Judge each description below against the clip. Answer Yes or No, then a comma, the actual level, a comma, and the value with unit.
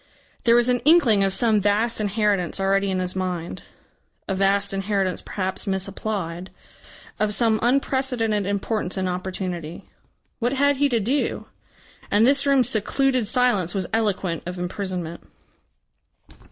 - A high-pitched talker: Yes, high, 205 Hz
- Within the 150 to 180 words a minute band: No, slow, 135 wpm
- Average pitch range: Yes, average, 4.0 semitones